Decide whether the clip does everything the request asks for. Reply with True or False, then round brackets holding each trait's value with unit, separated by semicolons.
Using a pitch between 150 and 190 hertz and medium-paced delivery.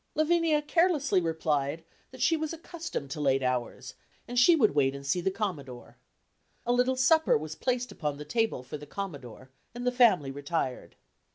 True (185 Hz; 175 wpm)